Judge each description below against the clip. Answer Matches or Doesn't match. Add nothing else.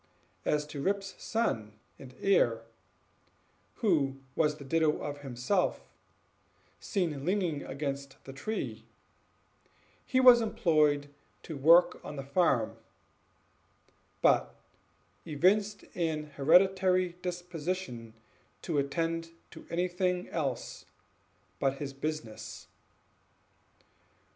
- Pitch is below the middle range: Doesn't match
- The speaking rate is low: Matches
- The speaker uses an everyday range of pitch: Matches